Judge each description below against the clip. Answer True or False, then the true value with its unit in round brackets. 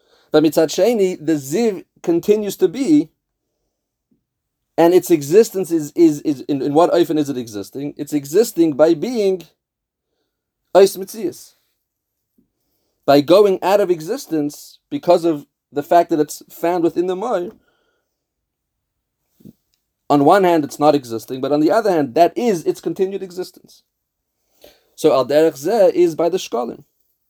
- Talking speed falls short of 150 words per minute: True (140 wpm)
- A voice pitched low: False (170 Hz)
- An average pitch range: True (5.0 semitones)